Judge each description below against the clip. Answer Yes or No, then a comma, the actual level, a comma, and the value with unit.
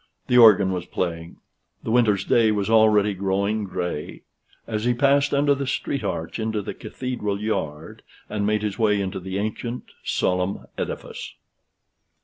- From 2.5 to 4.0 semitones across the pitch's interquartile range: Yes, average, 3.2 semitones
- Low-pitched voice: Yes, low, 105 Hz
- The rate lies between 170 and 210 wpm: No, average, 150 wpm